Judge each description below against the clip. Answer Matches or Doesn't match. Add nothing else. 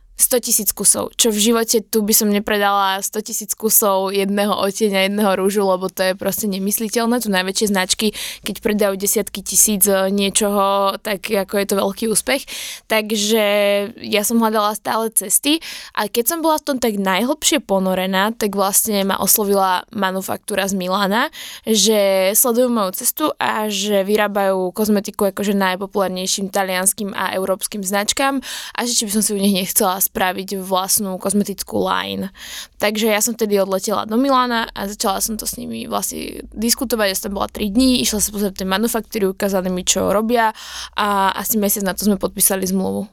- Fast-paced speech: Matches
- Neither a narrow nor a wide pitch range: Doesn't match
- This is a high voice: Matches